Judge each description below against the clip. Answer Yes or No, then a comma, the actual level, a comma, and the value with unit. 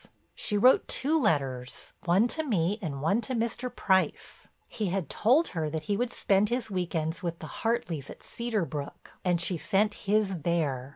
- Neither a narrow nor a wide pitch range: No, wide, 5.7 semitones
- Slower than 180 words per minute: No, average, 185 wpm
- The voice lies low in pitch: No, high, 190 Hz